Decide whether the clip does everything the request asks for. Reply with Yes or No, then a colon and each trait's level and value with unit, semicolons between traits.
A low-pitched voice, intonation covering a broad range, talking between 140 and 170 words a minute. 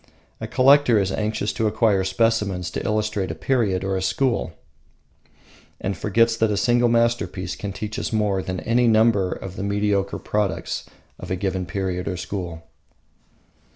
No: low, 105 Hz; average, 3.2 semitones; average, 160 wpm